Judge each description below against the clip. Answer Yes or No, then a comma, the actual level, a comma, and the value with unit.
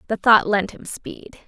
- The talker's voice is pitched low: No, high, 210 Hz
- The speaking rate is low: No, fast, 205 wpm